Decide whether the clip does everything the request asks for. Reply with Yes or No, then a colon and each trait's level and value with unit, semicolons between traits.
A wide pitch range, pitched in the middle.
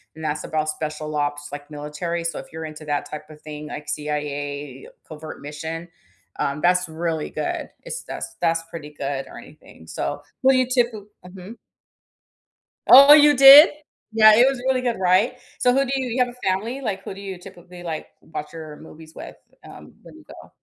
Yes: wide, 6.7 semitones; medium, 165 Hz